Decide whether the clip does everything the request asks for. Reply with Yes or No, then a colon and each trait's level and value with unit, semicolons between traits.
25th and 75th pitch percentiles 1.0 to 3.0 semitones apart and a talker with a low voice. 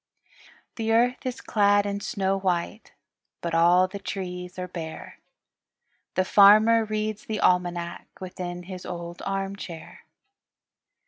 No: average, 2.7 semitones; high, 190 Hz